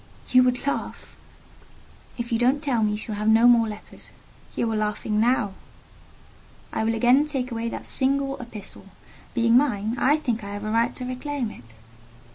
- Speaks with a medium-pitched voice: No, high, 235 Hz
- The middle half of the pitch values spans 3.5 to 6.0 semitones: No, average, 2.8 semitones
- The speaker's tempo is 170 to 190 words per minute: Yes, average, 180 wpm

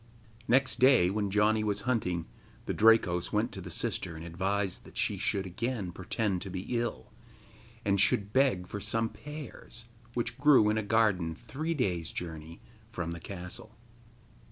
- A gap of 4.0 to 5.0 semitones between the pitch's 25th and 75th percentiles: Yes, average, 4.3 semitones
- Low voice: Yes, low, 105 Hz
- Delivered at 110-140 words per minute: No, average, 160 wpm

